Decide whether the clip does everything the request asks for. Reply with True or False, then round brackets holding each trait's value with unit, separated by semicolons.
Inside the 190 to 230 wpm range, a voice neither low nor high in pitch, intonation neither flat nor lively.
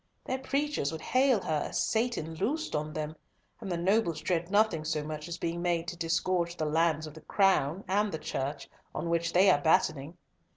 True (200 wpm; 170 Hz; 4.0 semitones)